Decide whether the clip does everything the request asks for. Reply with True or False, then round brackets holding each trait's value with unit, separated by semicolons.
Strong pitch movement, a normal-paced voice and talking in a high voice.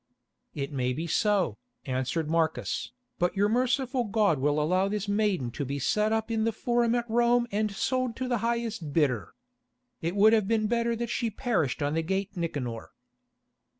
True (7.0 semitones; 180 wpm; 205 Hz)